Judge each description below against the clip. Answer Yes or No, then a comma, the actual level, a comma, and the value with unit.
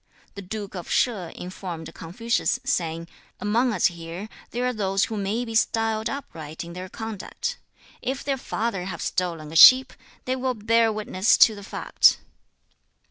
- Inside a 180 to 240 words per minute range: No, average, 160 wpm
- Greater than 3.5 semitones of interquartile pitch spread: Yes, average, 4.5 semitones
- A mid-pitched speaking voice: No, high, 210 Hz